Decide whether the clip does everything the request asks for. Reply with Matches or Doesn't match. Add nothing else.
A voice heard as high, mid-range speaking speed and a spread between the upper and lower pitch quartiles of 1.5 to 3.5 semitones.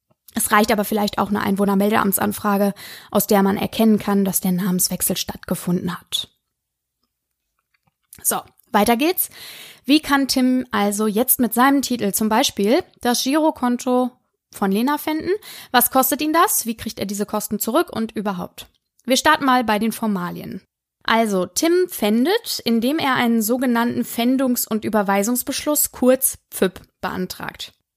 Doesn't match